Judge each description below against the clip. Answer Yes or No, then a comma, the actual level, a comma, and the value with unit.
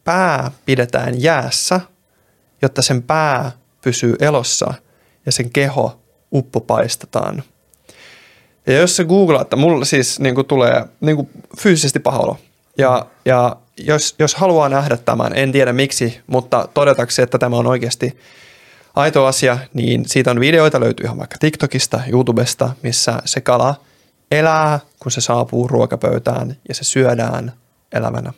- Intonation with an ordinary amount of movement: Yes, average, 3.0 semitones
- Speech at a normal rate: Yes, average, 135 wpm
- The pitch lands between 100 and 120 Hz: No, low, 135 Hz